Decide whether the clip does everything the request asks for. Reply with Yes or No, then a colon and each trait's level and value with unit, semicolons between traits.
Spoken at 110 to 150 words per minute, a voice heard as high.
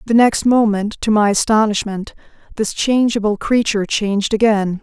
Yes: slow, 135 wpm; high, 215 Hz